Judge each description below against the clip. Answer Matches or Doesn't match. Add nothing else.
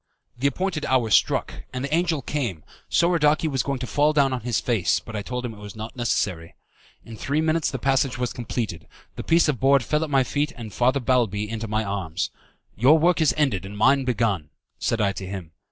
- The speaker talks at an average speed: Doesn't match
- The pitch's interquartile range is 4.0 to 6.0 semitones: Matches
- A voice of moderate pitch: Doesn't match